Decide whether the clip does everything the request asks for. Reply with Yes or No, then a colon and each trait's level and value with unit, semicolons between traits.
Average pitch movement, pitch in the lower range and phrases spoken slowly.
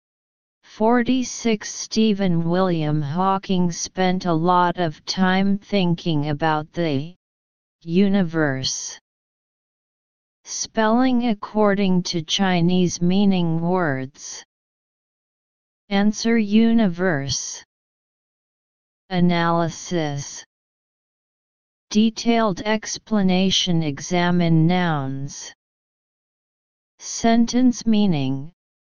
No: average, 4.2 semitones; medium, 180 Hz; slow, 60 wpm